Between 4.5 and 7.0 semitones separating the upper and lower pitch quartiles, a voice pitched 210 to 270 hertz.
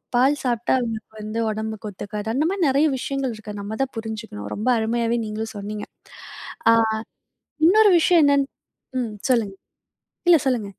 No: average, 4.1 semitones; high, 230 Hz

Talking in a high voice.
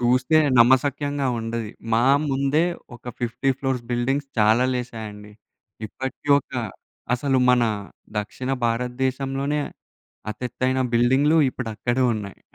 No: low, 125 Hz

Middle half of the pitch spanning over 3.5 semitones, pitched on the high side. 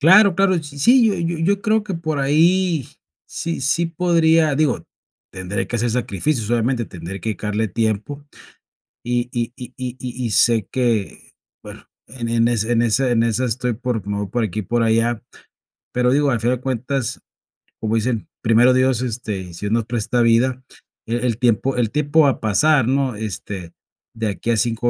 No: average, 4.1 semitones; low, 120 Hz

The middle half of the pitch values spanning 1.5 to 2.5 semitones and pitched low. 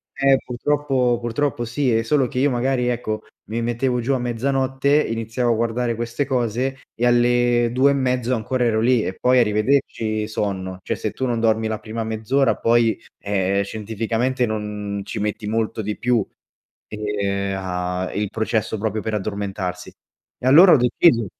No: average, 2.9 semitones; low, 115 Hz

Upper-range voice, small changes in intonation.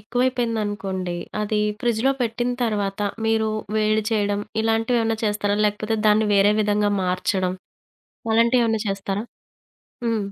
Yes: high, 215 Hz; narrow, 1.8 semitones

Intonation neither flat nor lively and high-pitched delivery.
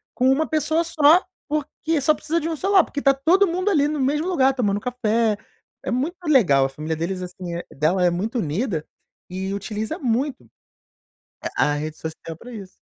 No: wide, 8.9 semitones; very high, 250 Hz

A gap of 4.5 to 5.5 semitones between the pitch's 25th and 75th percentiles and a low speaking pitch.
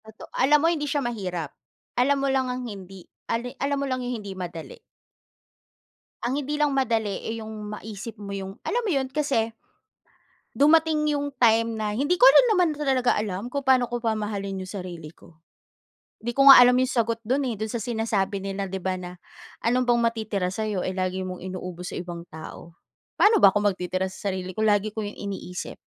No: average, 5.2 semitones; high, 220 Hz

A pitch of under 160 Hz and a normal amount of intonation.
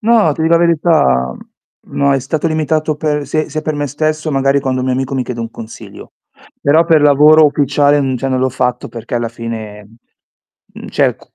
Yes: medium, 140 Hz; average, 3.5 semitones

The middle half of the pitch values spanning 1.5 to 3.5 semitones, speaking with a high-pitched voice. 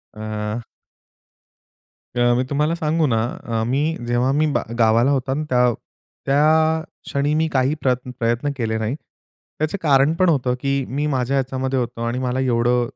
No: average, 2.9 semitones; low, 130 Hz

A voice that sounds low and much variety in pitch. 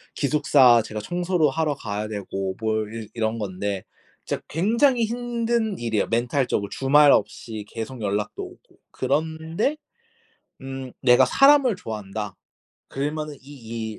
Yes: low, 130 Hz; wide, 6.7 semitones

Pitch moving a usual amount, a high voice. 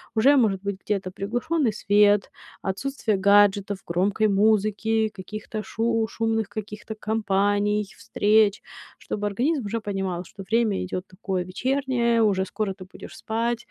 No: narrow, 2.3 semitones; high, 210 Hz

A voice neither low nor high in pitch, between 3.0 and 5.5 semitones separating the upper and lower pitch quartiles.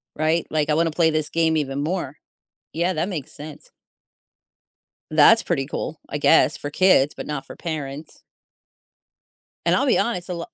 No: medium, 155 Hz; narrow, 2.5 semitones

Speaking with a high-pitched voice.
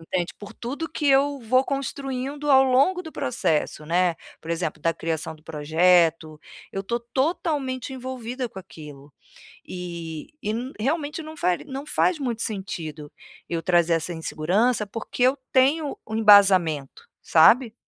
Yes: high, 220 Hz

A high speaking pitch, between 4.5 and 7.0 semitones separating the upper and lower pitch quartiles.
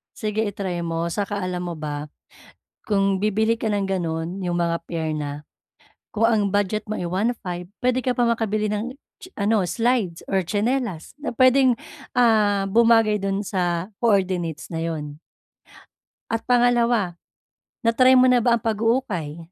Yes: high, 205 Hz; average, 4.8 semitones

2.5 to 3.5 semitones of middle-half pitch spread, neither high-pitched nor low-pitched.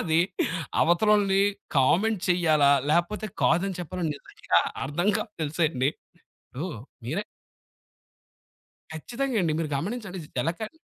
No: average, 5.0 semitones; medium, 175 Hz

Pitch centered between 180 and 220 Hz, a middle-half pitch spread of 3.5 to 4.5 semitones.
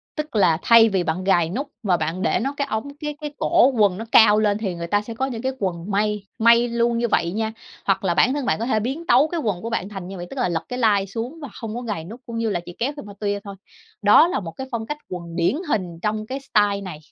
Yes: high, 215 Hz; average, 4.1 semitones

